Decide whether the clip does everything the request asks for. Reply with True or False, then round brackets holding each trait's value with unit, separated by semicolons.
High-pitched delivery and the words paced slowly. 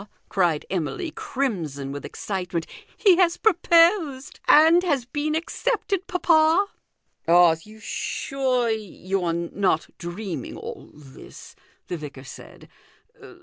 True (245 Hz; 120 wpm)